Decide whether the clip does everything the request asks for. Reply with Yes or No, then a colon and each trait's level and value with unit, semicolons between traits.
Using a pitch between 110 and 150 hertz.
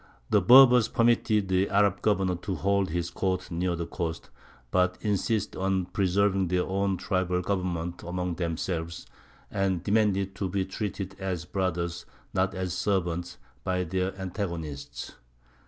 No: very low, 95 Hz